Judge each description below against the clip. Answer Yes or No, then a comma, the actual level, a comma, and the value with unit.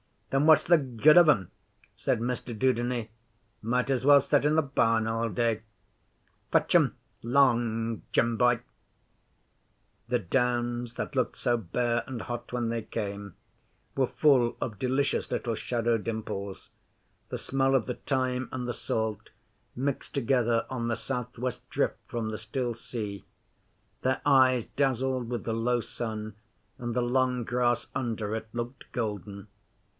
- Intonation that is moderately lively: No, narrow, 2.2 semitones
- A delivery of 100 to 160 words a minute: Yes, average, 150 wpm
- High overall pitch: No, low, 120 Hz